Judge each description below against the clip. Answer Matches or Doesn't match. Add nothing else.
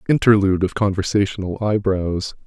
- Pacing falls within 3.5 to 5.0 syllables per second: Doesn't match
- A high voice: Doesn't match